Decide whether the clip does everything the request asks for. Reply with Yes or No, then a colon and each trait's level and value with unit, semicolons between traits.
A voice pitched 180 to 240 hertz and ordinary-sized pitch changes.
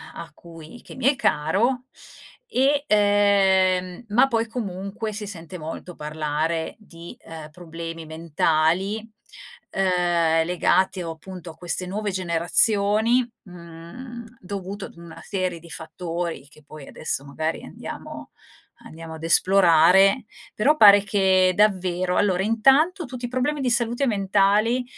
Yes: medium, 185 Hz; average, 4.4 semitones